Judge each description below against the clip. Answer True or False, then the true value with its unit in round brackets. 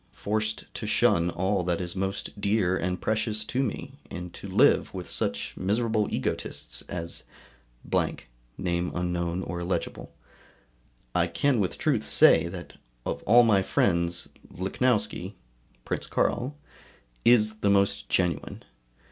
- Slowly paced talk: True (120 wpm)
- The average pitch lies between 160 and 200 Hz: False (95 Hz)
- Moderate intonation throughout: True (3.8 semitones)